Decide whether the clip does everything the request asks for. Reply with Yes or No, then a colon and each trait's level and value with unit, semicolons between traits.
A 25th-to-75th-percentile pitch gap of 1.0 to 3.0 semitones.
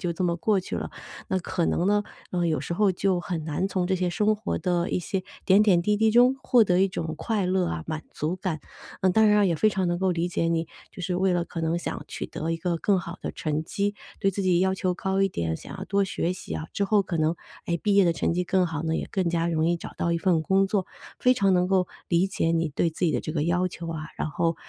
Yes: narrow, 2.5 semitones